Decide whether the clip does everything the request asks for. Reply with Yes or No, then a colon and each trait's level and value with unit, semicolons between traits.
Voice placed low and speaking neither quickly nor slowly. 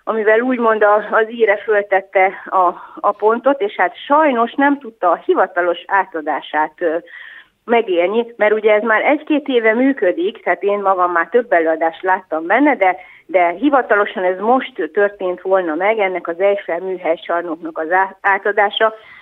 No: high, 200 Hz; average, 145 wpm